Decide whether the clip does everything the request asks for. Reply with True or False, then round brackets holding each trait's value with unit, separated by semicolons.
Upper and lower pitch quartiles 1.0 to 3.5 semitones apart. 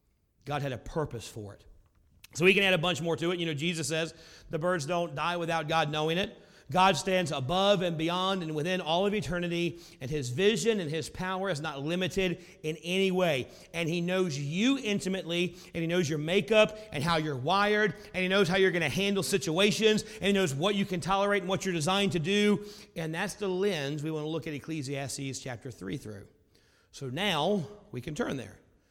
False (4.2 semitones)